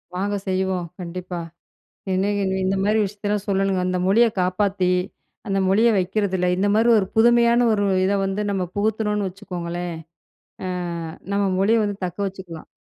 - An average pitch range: No, narrow, 2.2 semitones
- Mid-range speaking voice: No, high, 195 Hz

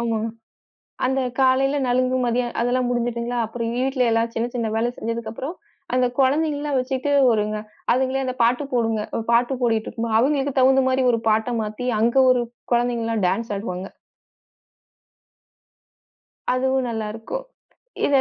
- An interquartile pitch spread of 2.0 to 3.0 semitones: Yes, narrow, 2.4 semitones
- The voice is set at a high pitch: Yes, high, 245 Hz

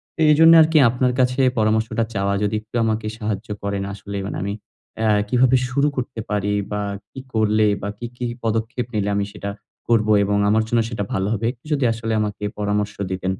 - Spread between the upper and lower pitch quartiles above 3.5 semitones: No, average, 2.8 semitones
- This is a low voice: Yes, low, 110 Hz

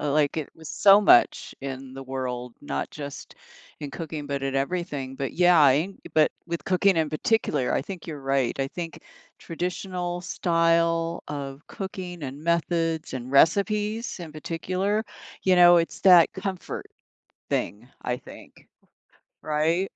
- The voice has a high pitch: No, medium, 165 Hz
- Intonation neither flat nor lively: Yes, average, 4.4 semitones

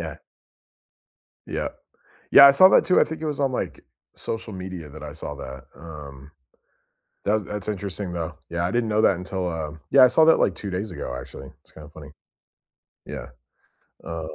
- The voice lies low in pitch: Yes, very low, 90 Hz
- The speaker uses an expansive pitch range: Yes, wide, 5.7 semitones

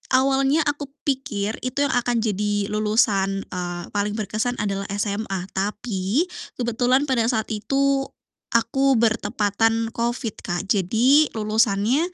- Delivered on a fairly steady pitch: No, average, 4.0 semitones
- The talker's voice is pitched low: No, high, 225 Hz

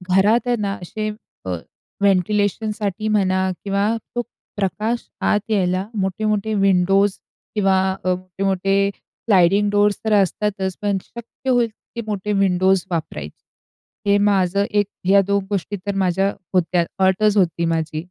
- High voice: Yes, high, 195 Hz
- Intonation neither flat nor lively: No, narrow, 2.0 semitones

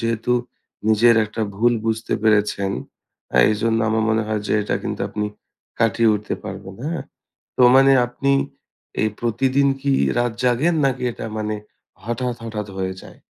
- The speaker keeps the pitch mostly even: Yes, narrow, 2.3 semitones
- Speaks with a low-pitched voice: Yes, low, 115 Hz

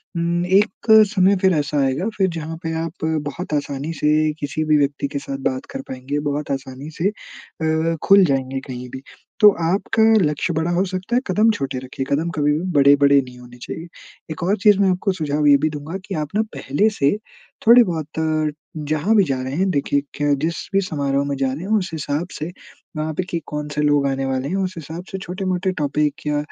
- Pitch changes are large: No, average, 4.3 semitones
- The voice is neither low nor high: Yes, medium, 155 Hz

